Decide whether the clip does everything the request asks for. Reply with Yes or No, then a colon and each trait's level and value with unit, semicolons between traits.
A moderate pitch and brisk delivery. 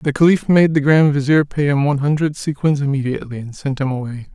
Yes: medium, 145 Hz; fast, 220 wpm